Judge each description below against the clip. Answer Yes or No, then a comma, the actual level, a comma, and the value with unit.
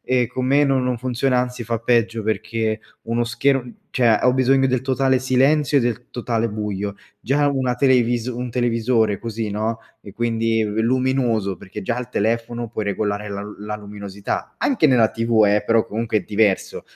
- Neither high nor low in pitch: No, low, 115 Hz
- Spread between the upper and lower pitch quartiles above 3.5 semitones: No, average, 2.7 semitones